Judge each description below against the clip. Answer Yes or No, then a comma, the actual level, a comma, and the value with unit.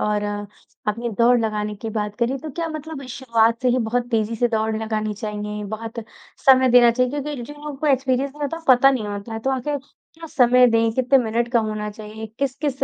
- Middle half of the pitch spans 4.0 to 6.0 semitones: No, average, 3.5 semitones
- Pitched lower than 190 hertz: No, high, 240 Hz